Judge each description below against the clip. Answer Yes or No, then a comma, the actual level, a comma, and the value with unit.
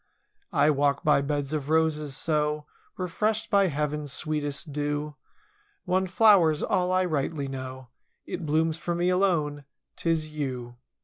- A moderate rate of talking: No, slow, 130 wpm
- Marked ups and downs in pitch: No, average, 3.1 semitones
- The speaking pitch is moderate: Yes, medium, 150 Hz